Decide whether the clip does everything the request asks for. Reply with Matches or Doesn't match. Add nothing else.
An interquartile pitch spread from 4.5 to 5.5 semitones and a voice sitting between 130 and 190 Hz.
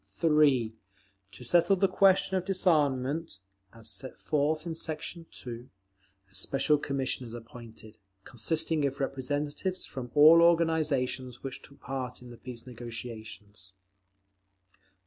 Matches